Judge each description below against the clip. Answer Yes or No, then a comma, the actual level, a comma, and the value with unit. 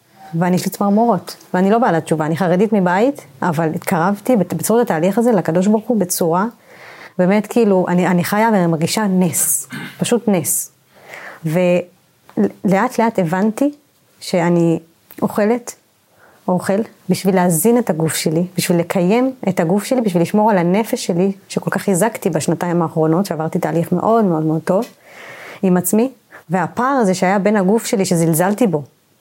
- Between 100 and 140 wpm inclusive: No, fast, 150 wpm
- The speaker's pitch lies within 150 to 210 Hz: Yes, medium, 185 Hz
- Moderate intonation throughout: Yes, average, 3.9 semitones